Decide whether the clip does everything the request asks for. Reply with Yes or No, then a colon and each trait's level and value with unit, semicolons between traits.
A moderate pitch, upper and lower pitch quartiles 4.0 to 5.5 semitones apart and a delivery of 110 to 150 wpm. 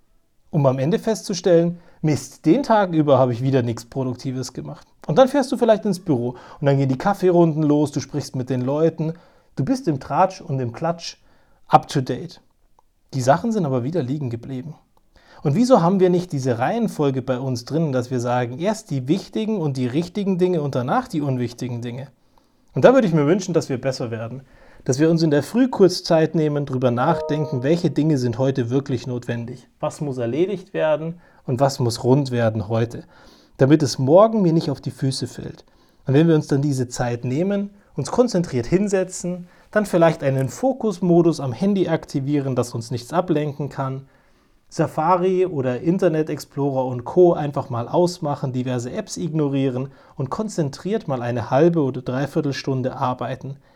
No: medium, 145 Hz; average, 5.0 semitones; average, 180 wpm